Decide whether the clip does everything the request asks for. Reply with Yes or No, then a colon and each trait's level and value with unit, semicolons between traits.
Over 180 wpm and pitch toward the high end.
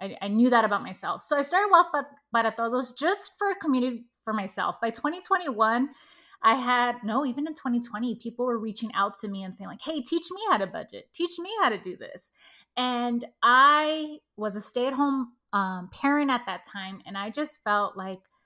Yes: average, 200 wpm; very high, 250 Hz